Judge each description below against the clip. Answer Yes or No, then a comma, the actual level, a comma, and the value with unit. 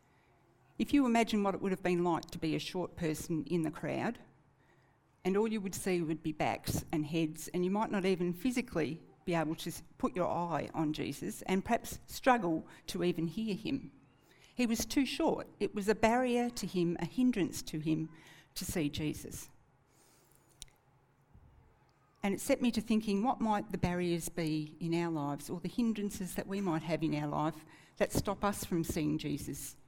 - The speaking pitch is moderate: Yes, medium, 175 Hz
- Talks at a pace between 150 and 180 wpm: No, average, 190 wpm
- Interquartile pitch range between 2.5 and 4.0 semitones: No, average, 4.6 semitones